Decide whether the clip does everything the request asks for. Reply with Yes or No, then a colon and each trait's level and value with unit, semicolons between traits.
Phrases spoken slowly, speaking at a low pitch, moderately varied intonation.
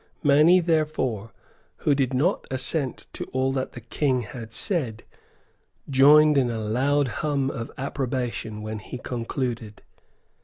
Yes: slow, 130 wpm; low, 130 Hz; average, 3.8 semitones